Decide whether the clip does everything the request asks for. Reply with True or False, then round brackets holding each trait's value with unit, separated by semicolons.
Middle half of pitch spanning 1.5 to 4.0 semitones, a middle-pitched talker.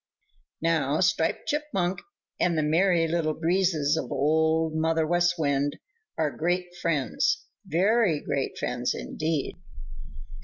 True (2.5 semitones; 160 Hz)